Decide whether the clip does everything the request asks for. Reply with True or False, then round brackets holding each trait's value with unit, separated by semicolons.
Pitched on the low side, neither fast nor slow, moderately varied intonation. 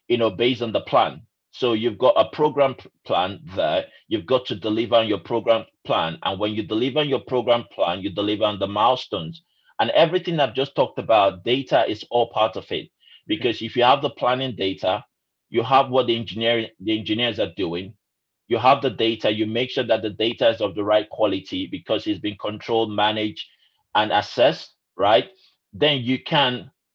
True (115 Hz; 195 wpm; 3.2 semitones)